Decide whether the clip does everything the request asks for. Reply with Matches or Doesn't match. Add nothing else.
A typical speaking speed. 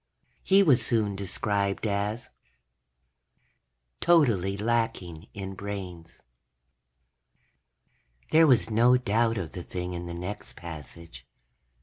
Doesn't match